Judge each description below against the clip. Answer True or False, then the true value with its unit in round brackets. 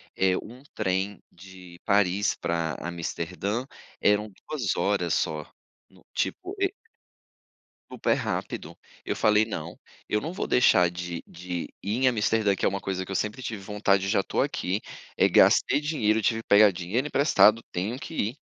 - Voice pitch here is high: False (100 Hz)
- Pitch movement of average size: True (3.6 semitones)